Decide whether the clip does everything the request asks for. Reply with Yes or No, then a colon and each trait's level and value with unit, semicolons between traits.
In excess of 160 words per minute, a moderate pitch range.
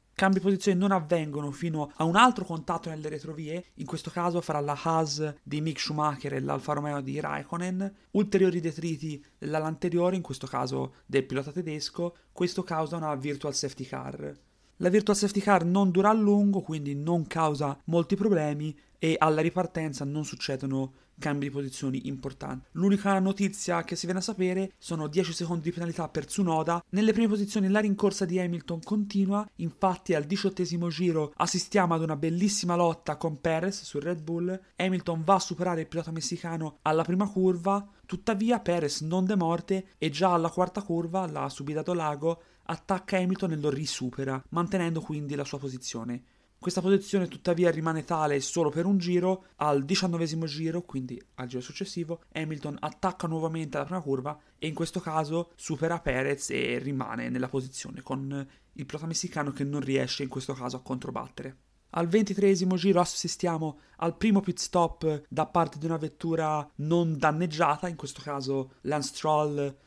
Yes: fast, 170 wpm; average, 3.7 semitones